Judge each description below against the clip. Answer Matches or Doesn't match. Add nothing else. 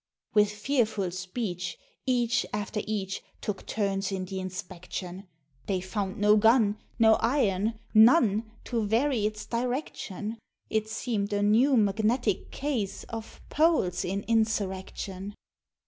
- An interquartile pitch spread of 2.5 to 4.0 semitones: Matches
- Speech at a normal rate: Doesn't match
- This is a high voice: Matches